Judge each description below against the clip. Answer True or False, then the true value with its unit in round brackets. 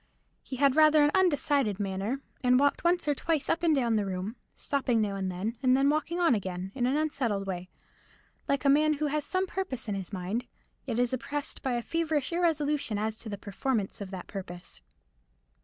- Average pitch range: False (6.7 semitones)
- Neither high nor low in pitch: False (260 Hz)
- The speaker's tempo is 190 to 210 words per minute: True (205 wpm)